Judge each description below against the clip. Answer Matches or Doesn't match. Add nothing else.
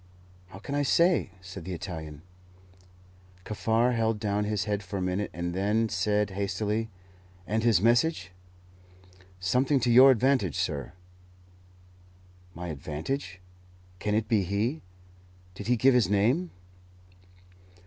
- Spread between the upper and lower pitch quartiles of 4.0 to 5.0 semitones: Matches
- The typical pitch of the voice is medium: Doesn't match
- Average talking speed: Doesn't match